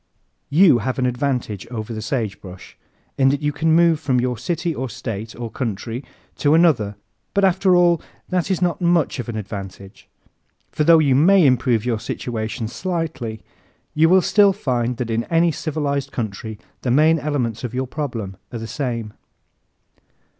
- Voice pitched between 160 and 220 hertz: No, low, 130 Hz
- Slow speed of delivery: No, average, 170 wpm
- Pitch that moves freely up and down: Yes, wide, 6.1 semitones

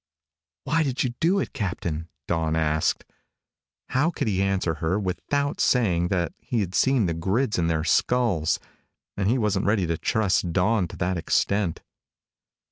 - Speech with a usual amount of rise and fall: No, wide, 6.2 semitones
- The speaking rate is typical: Yes, average, 155 wpm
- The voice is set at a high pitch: No, very low, 95 Hz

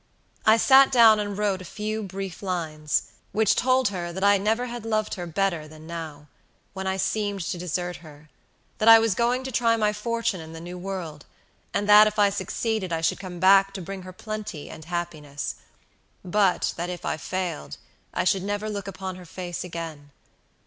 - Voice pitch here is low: No, high, 190 Hz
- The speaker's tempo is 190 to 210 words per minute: Yes, average, 195 wpm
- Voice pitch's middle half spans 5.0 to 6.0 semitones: No, average, 3.6 semitones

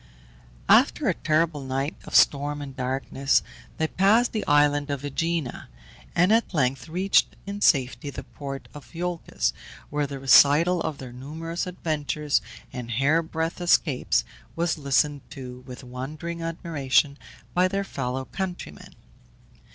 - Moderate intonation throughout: Yes, average, 3.7 semitones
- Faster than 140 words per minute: No, slow, 135 wpm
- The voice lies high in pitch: No, medium, 145 Hz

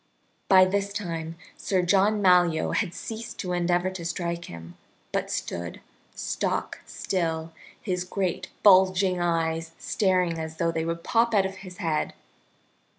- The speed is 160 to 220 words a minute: No, average, 145 wpm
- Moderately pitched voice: Yes, medium, 180 Hz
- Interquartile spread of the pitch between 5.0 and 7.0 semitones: No, narrow, 2.4 semitones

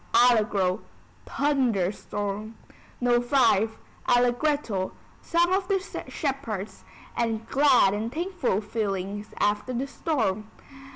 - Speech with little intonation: No, average, 5.0 semitones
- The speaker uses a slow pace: Yes, slow, 100 wpm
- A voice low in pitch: No, high, 230 Hz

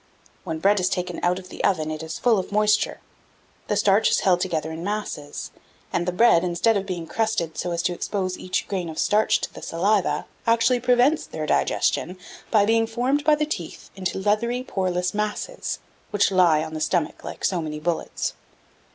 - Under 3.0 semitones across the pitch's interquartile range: No, average, 4.0 semitones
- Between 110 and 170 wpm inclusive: No, average, 195 wpm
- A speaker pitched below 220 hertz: Yes, high, 190 Hz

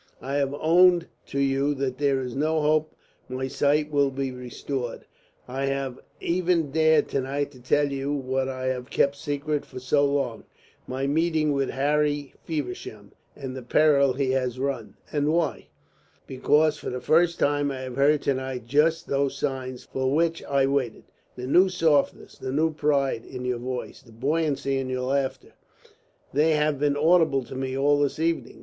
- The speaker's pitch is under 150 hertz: Yes, medium, 140 Hz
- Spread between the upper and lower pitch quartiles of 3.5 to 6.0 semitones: No, narrow, 2.4 semitones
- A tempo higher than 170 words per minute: Yes, average, 180 wpm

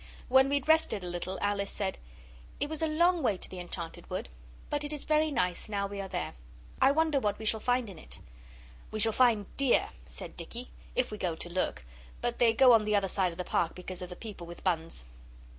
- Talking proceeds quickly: Yes, fast, 230 wpm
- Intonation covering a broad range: Yes, wide, 6.3 semitones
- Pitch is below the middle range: No, high, 210 Hz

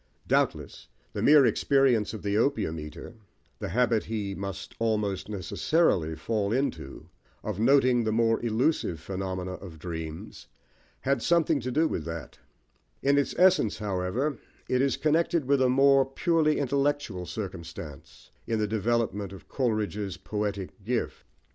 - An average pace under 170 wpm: Yes, average, 140 wpm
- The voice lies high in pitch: No, low, 110 Hz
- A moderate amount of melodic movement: No, wide, 6.1 semitones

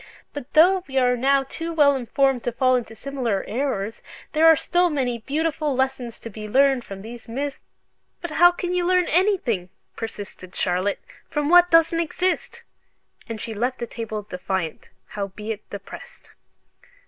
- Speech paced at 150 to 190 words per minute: Yes, average, 160 wpm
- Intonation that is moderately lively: No, wide, 6.1 semitones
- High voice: Yes, very high, 260 Hz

